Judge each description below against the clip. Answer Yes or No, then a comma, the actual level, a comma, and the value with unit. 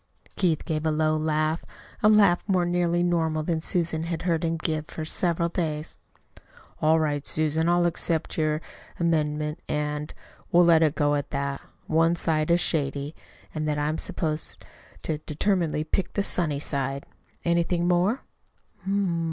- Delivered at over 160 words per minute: No, average, 150 wpm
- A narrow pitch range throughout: Yes, narrow, 2.1 semitones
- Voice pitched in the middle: Yes, medium, 160 Hz